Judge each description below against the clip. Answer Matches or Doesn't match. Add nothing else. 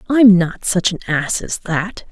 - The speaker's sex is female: Matches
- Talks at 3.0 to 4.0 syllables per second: Matches